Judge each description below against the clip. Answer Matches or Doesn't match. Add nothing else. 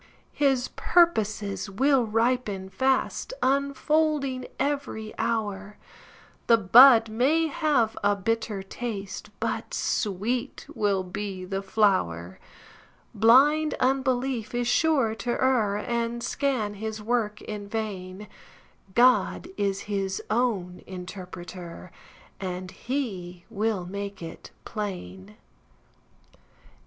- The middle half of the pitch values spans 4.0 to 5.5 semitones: Matches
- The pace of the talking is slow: Matches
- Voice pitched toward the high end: Matches